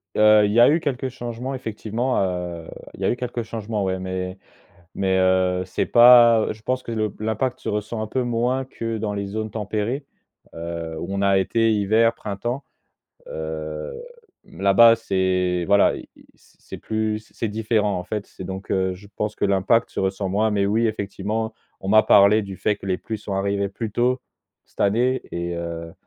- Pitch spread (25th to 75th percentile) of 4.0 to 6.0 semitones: No, average, 3.2 semitones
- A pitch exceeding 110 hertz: No, low, 105 Hz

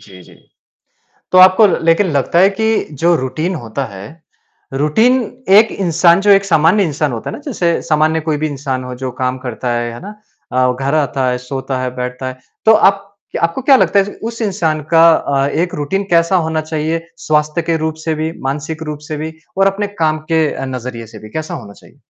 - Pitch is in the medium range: Yes, medium, 155 Hz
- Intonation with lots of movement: No, average, 5.0 semitones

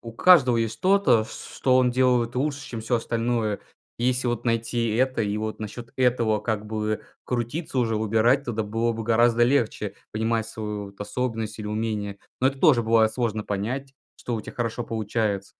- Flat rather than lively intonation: Yes, narrow, 2.3 semitones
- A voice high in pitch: No, low, 115 Hz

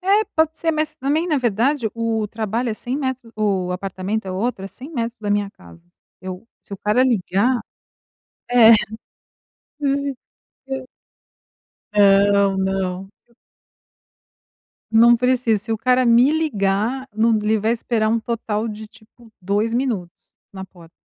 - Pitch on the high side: Yes, high, 225 Hz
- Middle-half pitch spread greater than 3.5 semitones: Yes, average, 4.1 semitones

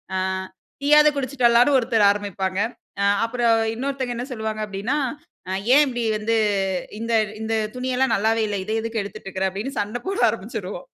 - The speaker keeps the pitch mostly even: No, average, 3.6 semitones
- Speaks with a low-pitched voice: No, high, 230 Hz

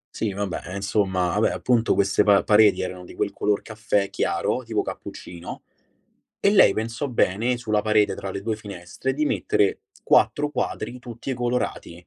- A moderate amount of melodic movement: Yes, average, 3.3 semitones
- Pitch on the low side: Yes, low, 105 Hz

